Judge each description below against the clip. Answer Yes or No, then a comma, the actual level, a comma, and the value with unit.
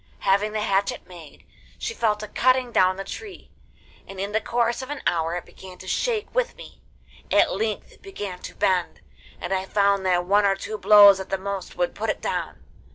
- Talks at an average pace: No, fast, 210 wpm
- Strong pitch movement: No, average, 3.8 semitones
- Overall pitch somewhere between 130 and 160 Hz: No, high, 200 Hz